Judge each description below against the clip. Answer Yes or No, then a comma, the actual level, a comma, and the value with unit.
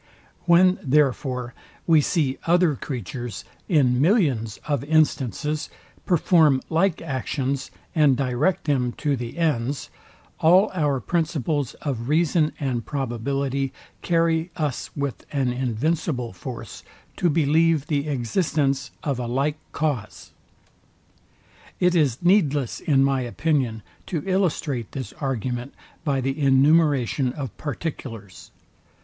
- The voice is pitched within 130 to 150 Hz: Yes, medium, 140 Hz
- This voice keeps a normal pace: No, slow, 115 wpm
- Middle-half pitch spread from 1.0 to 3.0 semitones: No, average, 4.0 semitones